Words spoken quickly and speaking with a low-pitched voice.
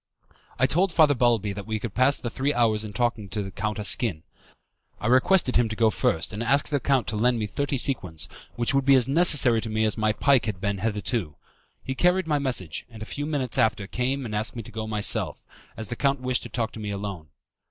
Yes: fast, 235 wpm; low, 115 Hz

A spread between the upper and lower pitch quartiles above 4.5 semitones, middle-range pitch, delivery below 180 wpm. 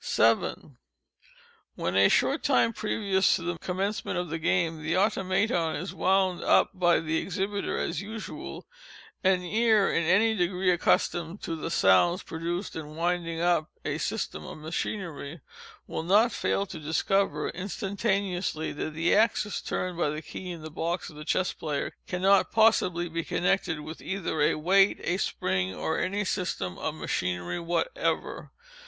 No: average, 3.5 semitones; medium, 175 Hz; average, 155 wpm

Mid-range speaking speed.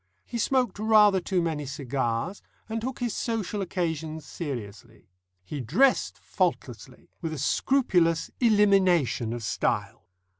No: slow, 120 wpm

